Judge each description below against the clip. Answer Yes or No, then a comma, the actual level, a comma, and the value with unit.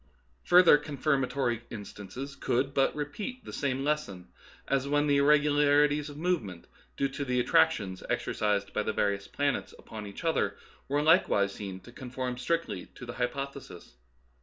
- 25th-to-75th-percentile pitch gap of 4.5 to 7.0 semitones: Yes, average, 5.2 semitones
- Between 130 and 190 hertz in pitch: Yes, low, 135 Hz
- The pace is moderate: Yes, average, 150 wpm